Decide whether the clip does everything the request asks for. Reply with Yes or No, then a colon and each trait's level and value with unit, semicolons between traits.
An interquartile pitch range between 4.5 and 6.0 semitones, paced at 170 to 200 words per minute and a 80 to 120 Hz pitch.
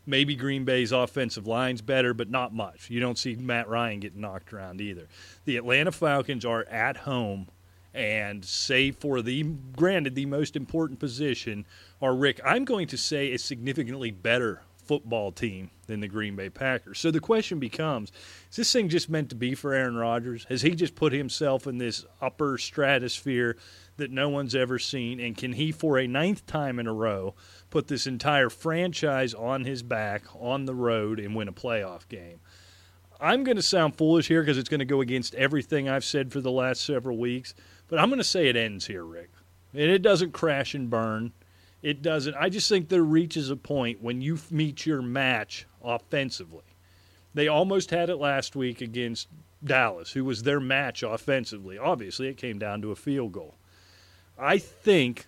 No: average, 5.1 semitones; average, 190 wpm; low, 130 Hz